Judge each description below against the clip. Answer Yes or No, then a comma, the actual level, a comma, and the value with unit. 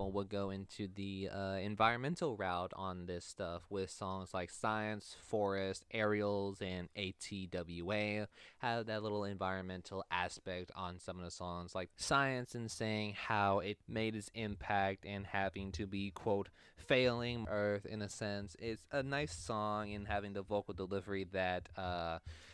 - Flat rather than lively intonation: Yes, narrow, 2.1 semitones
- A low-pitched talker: Yes, low, 100 Hz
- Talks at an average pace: Yes, average, 155 wpm